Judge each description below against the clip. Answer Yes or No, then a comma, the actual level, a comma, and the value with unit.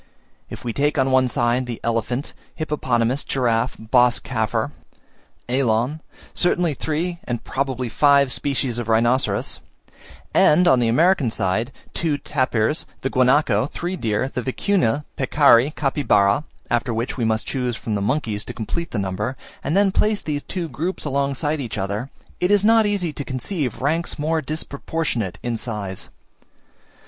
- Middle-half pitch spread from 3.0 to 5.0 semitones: Yes, average, 4.6 semitones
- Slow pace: No, average, 155 wpm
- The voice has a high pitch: No, low, 130 Hz